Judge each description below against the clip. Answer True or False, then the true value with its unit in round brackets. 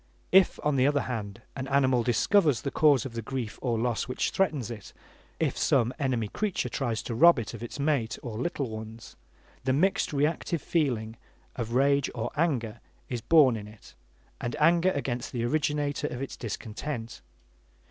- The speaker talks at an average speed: True (170 wpm)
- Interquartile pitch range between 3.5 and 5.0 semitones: True (4.2 semitones)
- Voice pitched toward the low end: True (130 Hz)